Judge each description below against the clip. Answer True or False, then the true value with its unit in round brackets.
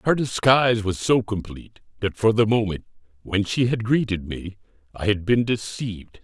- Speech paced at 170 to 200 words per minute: True (175 wpm)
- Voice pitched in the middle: False (105 Hz)